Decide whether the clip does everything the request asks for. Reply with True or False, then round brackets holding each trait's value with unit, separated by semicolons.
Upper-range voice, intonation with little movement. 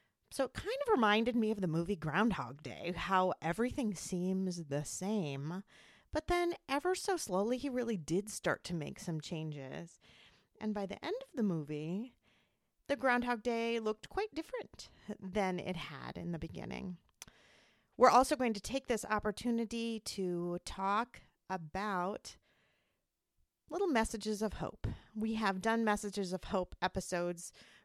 False (205 Hz; 4.9 semitones)